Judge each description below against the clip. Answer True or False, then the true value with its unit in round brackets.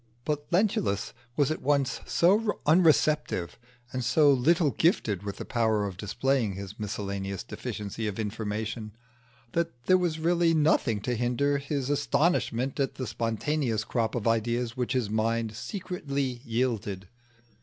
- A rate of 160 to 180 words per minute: False (140 wpm)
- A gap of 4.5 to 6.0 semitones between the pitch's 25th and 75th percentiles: True (5.2 semitones)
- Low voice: True (120 Hz)